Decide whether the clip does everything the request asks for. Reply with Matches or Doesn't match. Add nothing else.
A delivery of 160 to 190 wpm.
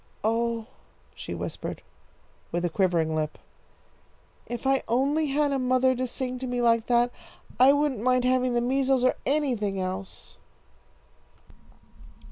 Doesn't match